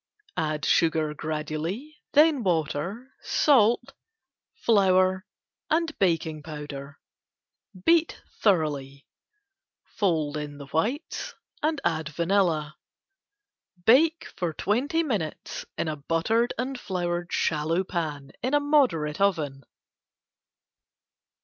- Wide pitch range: Yes, wide, 7.7 semitones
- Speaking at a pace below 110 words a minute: Yes, slow, 85 wpm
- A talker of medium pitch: Yes, medium, 175 Hz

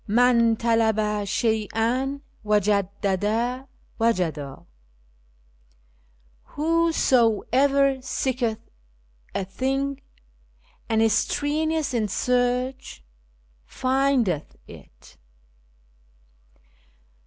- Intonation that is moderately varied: Yes, average, 4.0 semitones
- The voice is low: No, high, 235 Hz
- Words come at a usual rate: No, slow, 60 wpm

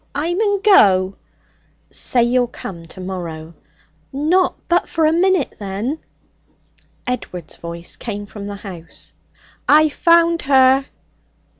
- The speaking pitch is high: Yes, very high, 250 Hz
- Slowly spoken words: Yes, slow, 115 wpm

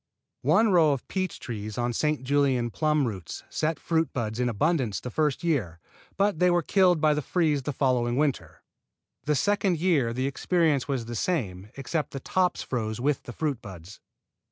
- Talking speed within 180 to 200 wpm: Yes, average, 190 wpm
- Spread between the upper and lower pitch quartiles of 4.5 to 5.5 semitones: Yes, average, 5.2 semitones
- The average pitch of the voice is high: No, medium, 140 Hz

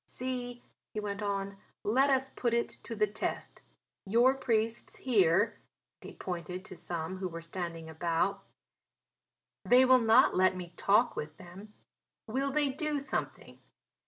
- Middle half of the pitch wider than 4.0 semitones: Yes, wide, 5.5 semitones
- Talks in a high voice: Yes, high, 210 Hz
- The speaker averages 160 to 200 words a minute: No, average, 150 wpm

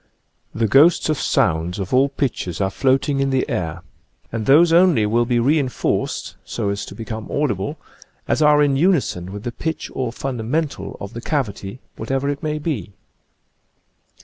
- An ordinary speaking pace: Yes, average, 175 wpm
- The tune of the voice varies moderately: No, wide, 5.8 semitones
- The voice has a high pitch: No, low, 130 Hz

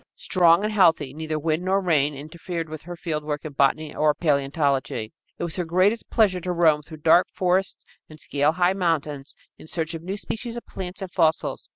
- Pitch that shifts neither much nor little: Yes, average, 3.3 semitones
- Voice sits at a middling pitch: Yes, medium, 165 Hz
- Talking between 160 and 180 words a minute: No, average, 195 wpm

